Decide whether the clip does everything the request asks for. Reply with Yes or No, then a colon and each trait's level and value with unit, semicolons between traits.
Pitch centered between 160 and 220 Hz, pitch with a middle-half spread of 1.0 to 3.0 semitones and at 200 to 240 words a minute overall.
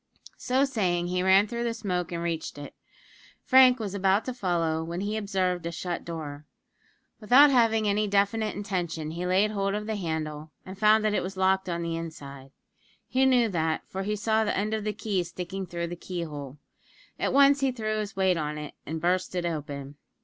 No: high, 190 Hz; average, 4.2 semitones; fast, 205 wpm